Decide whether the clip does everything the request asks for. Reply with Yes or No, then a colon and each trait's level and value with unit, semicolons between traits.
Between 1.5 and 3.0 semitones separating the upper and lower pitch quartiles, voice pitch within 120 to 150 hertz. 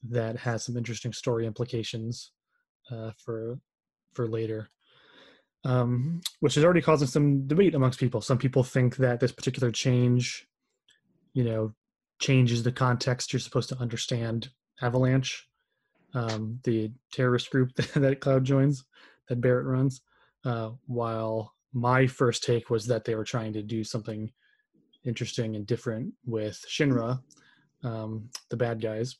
Yes: narrow, 2.5 semitones; low, 125 Hz